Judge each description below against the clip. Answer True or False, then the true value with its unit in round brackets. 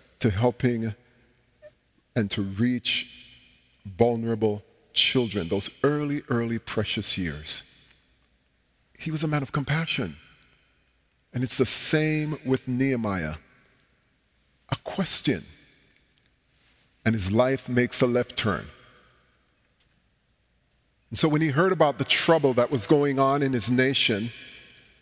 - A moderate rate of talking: False (115 wpm)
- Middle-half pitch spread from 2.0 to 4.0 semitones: False (4.7 semitones)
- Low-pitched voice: True (120 Hz)